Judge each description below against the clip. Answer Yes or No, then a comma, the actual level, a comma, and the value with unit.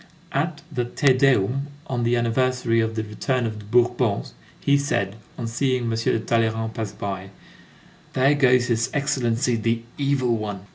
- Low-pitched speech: Yes, low, 120 Hz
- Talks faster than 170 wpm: No, average, 160 wpm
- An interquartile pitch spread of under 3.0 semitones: Yes, narrow, 2.5 semitones